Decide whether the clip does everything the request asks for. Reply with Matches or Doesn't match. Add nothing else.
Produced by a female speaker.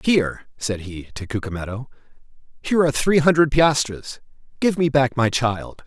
Doesn't match